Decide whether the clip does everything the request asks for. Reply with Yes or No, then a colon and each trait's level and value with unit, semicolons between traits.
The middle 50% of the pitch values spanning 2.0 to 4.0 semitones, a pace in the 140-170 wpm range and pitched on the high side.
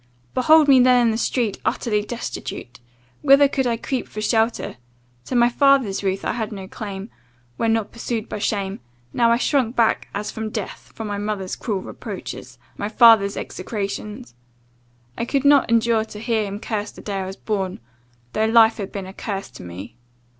No: average, 2.9 semitones; average, 185 wpm; high, 220 Hz